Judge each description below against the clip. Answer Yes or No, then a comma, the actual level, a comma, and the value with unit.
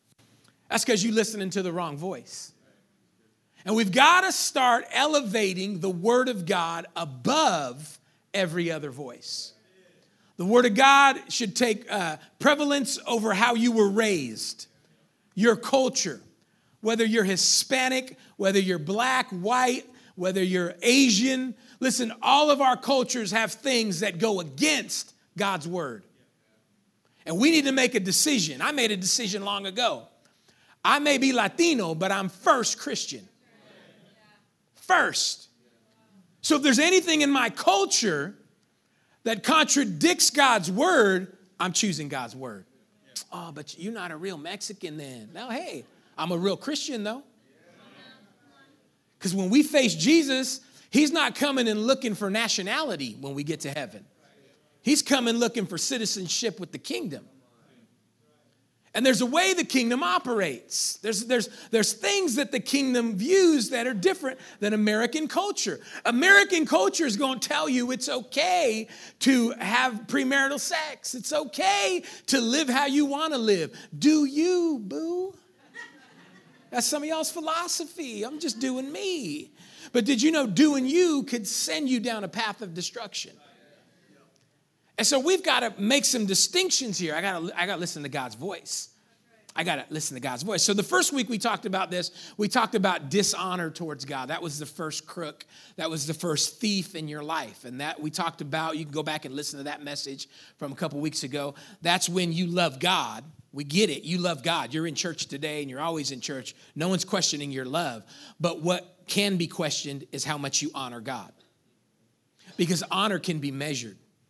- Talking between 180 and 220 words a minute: No, average, 165 wpm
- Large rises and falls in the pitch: Yes, wide, 7.7 semitones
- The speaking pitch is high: Yes, high, 215 Hz